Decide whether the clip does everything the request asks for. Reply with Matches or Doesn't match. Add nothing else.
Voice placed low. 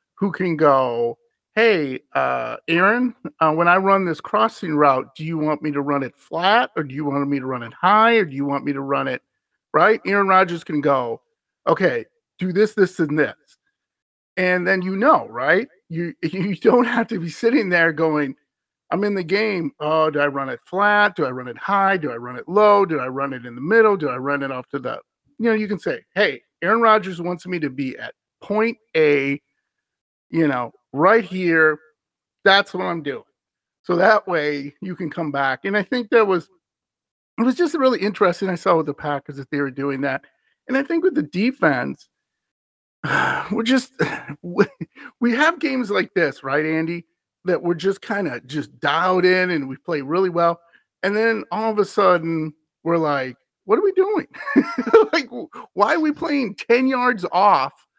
Doesn't match